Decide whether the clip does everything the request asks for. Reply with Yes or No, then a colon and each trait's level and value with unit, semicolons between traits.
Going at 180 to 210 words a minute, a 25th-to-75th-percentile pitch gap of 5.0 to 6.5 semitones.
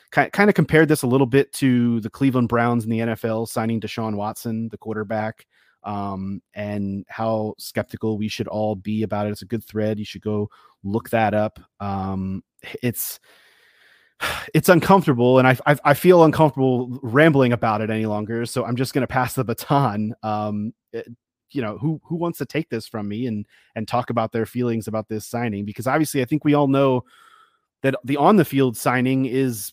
No: average, 195 wpm; average, 3.9 semitones